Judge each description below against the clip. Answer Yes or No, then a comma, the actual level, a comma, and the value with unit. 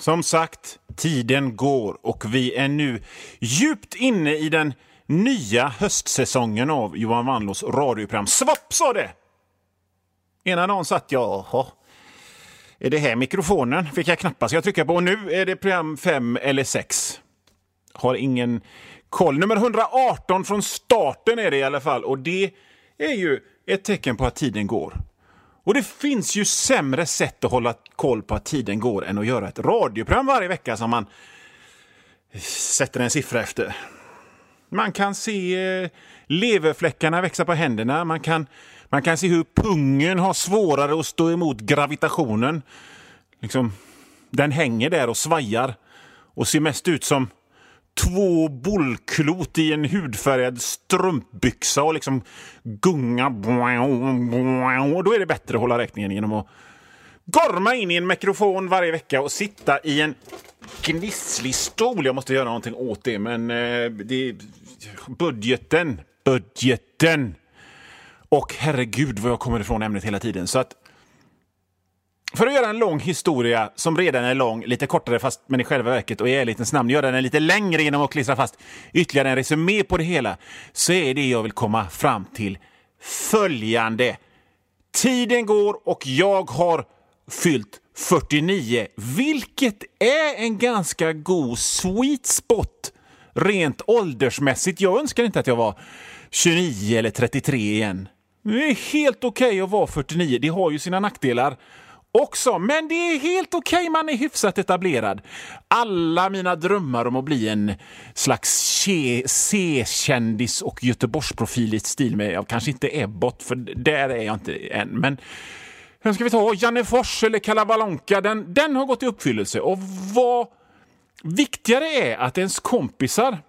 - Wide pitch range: Yes, wide, 8.0 semitones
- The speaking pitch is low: No, medium, 155 Hz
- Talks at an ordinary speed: Yes, average, 155 wpm